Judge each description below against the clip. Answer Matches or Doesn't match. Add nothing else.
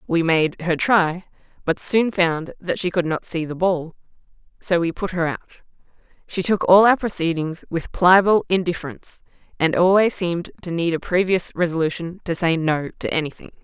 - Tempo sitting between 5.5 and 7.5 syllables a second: Doesn't match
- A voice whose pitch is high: Doesn't match